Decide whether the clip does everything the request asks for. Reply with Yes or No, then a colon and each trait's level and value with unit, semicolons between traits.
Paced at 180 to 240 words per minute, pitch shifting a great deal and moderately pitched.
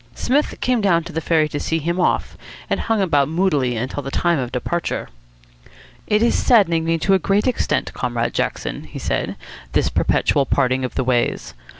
Yes: average, 190 wpm; wide, 5.9 semitones; medium, 165 Hz